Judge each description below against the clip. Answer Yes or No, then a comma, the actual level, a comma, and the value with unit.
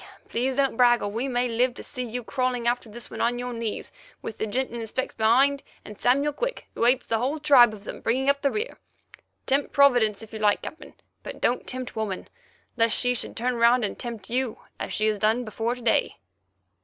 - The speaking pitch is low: No, high, 245 Hz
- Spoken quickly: Yes, fast, 225 wpm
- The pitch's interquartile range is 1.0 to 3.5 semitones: Yes, narrow, 2.5 semitones